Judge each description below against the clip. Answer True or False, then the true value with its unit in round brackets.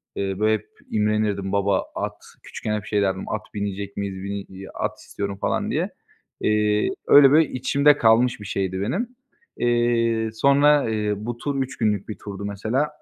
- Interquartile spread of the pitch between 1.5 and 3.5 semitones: True (3.2 semitones)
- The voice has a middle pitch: False (105 Hz)